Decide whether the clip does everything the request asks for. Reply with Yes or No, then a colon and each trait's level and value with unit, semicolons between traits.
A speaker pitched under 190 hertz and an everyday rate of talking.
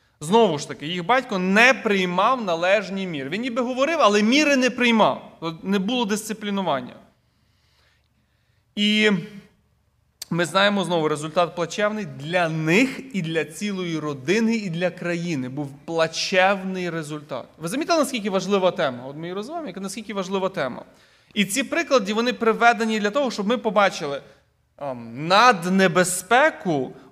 No: high, 195 Hz; average, 130 wpm